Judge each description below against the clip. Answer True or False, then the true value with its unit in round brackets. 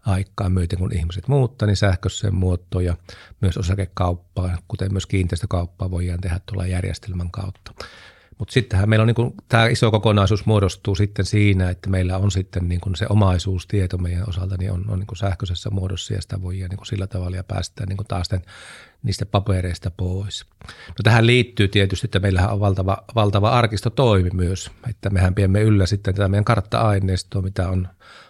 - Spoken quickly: True (175 wpm)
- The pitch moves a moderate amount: False (2.0 semitones)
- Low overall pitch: True (95 Hz)